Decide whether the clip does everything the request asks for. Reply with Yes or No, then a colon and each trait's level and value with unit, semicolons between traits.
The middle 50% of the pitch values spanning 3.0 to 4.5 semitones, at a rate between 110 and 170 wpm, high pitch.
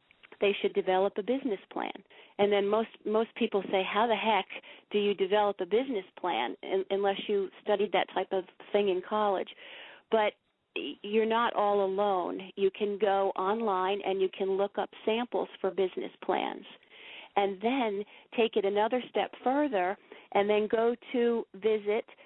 No: narrow, 2.4 semitones; average, 165 wpm; high, 205 Hz